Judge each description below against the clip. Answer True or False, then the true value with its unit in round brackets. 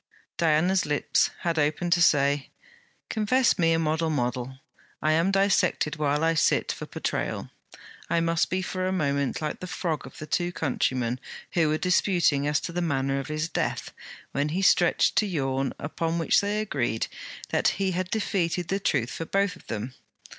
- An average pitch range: True (4.0 semitones)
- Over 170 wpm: True (180 wpm)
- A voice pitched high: False (165 Hz)